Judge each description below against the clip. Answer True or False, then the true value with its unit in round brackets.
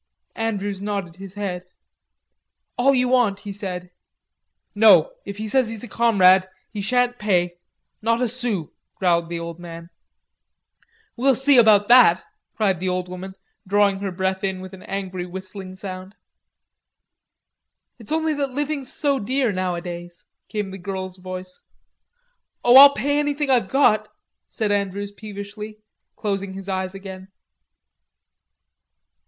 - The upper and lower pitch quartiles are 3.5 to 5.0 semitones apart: True (3.8 semitones)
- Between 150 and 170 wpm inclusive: False (135 wpm)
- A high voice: True (200 Hz)